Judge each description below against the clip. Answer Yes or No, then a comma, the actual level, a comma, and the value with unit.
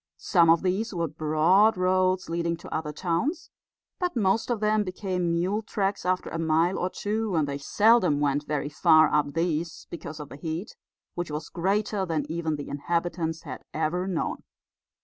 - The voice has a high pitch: No, medium, 170 Hz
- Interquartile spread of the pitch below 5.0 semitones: Yes, average, 3.4 semitones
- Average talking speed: Yes, average, 175 wpm